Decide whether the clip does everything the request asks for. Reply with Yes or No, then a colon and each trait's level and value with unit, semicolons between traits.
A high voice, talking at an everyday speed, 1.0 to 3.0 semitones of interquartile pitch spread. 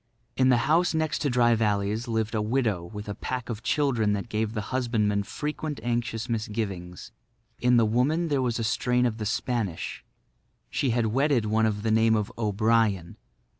No: low, 115 Hz; average, 180 wpm; average, 2.7 semitones